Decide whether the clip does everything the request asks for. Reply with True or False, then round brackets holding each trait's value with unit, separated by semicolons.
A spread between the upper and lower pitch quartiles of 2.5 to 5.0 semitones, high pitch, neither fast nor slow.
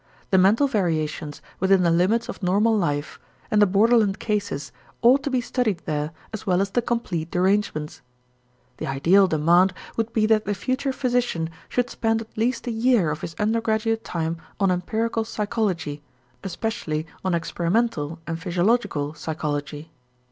False (5.4 semitones; 195 Hz; 155 wpm)